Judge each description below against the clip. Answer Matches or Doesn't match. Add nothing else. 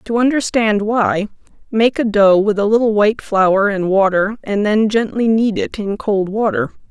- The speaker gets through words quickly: Doesn't match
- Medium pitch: Doesn't match